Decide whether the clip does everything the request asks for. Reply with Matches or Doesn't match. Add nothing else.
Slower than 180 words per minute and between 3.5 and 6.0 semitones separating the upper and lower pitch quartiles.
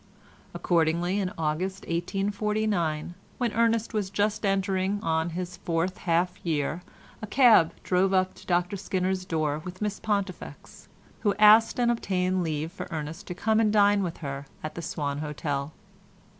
Matches